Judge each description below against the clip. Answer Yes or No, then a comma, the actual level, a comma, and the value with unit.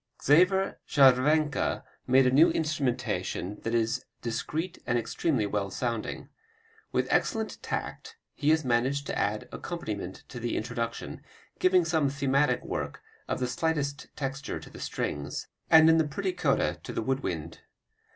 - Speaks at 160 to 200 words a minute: No, average, 150 wpm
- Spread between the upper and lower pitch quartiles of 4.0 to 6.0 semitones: Yes, average, 5.3 semitones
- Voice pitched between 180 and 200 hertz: No, low, 135 Hz